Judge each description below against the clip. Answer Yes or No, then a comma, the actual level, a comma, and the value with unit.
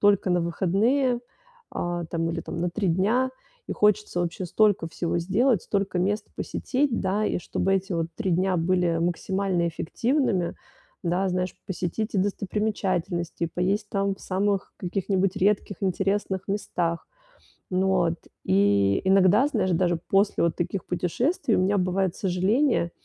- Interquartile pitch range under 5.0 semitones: Yes, average, 2.8 semitones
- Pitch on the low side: No, high, 190 Hz